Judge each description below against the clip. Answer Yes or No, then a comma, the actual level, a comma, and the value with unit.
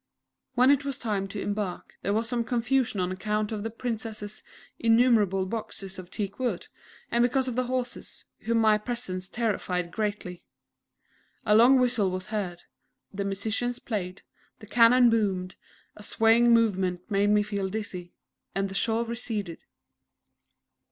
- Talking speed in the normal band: Yes, average, 150 wpm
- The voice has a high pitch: Yes, high, 215 Hz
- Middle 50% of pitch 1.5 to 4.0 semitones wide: Yes, average, 3.2 semitones